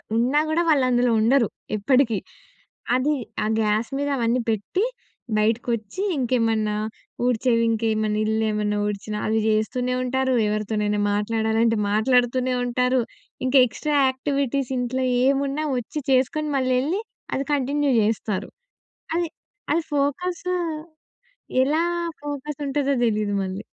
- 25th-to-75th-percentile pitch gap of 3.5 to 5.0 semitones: Yes, average, 4.1 semitones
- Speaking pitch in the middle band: No, very high, 250 Hz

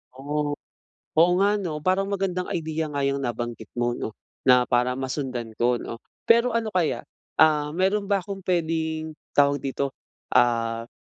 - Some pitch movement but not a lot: No, wide, 6.3 semitones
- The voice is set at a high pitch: No, medium, 150 Hz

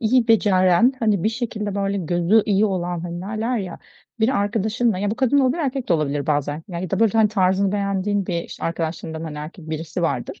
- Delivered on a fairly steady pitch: No, average, 4.4 semitones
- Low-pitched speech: No, high, 195 Hz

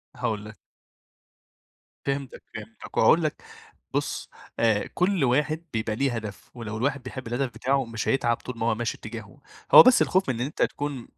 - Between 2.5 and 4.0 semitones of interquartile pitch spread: Yes, average, 3.6 semitones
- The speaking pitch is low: Yes, low, 120 Hz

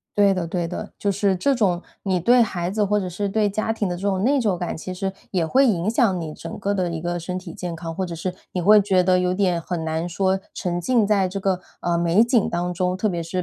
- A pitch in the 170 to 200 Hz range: Yes, medium, 185 Hz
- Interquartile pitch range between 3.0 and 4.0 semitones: No, narrow, 2.6 semitones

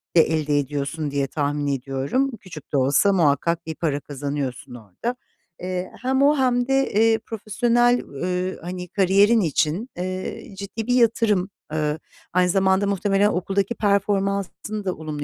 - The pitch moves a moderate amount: No, wide, 6.1 semitones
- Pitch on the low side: No, medium, 185 Hz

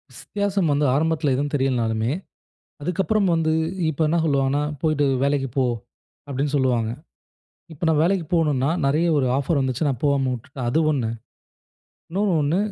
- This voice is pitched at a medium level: Yes, medium, 145 Hz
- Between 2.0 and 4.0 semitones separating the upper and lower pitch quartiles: Yes, average, 3.4 semitones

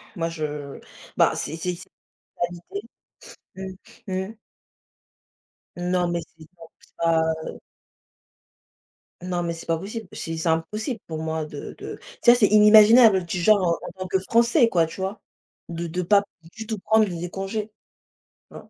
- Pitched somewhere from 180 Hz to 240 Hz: Yes, medium, 185 Hz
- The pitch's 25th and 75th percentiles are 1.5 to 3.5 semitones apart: No, average, 4.3 semitones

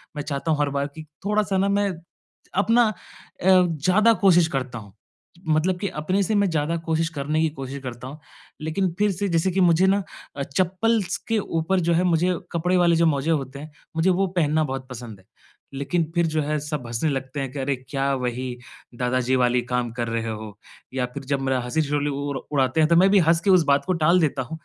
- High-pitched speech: No, medium, 155 Hz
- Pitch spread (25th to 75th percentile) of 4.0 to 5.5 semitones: Yes, average, 5.0 semitones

